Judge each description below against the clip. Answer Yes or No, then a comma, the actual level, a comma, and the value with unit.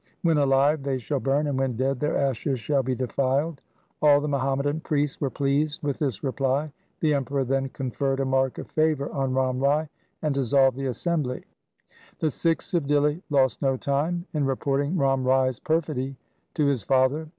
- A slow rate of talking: No, average, 180 wpm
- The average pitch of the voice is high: No, medium, 140 Hz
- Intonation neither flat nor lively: No, narrow, 2.0 semitones